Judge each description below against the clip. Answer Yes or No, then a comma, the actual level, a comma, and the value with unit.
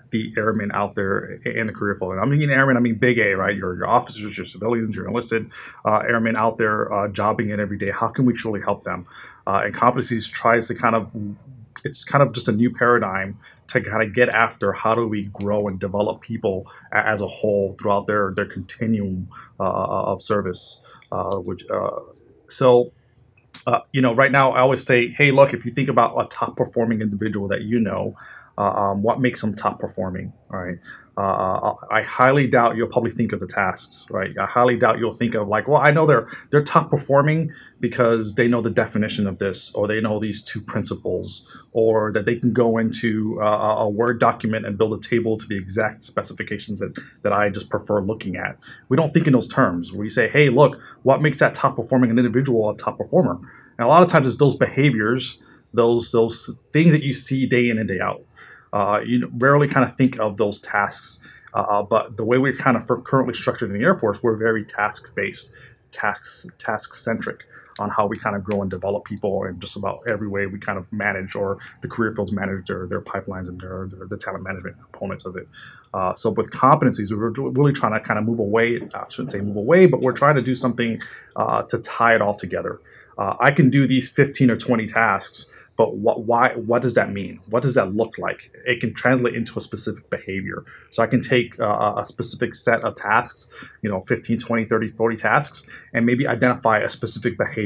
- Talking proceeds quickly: Yes, fast, 220 wpm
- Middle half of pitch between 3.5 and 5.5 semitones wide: No, average, 3.1 semitones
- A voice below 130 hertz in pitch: Yes, low, 115 Hz